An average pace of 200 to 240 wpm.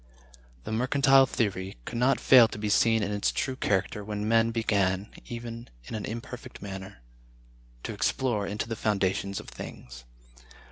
No: average, 155 wpm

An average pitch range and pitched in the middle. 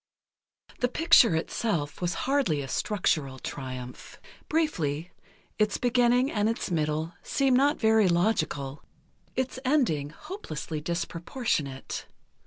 No: wide, 8.7 semitones; medium, 180 Hz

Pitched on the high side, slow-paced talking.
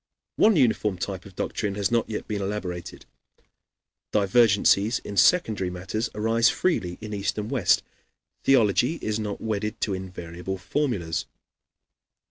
No: low, 105 Hz; slow, 130 wpm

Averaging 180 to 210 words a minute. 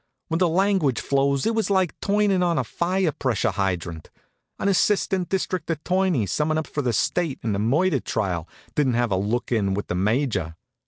Yes: average, 190 wpm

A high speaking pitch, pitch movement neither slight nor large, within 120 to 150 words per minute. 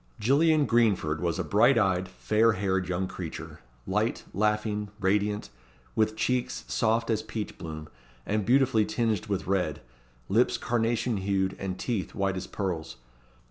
No: low, 105 Hz; average, 3.2 semitones; average, 140 wpm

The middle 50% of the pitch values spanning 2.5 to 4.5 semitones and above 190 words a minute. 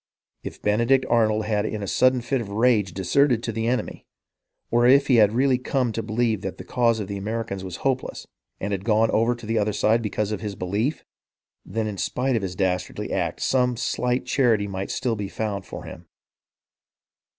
Yes: average, 3.2 semitones; average, 200 wpm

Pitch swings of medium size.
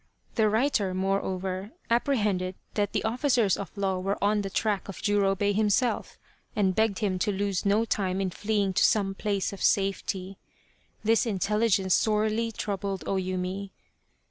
No: narrow, 2.0 semitones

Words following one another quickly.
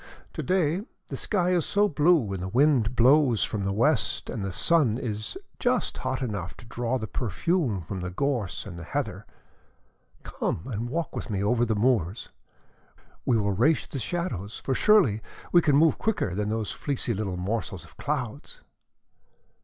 No: average, 175 wpm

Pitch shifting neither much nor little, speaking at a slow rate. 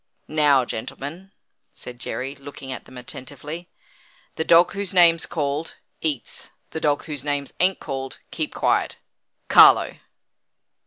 Yes: average, 3.6 semitones; slow, 125 wpm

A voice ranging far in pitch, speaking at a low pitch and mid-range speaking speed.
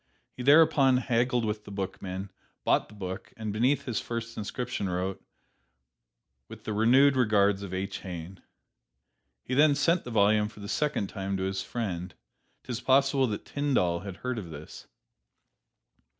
No: average, 4.8 semitones; low, 110 Hz; average, 160 wpm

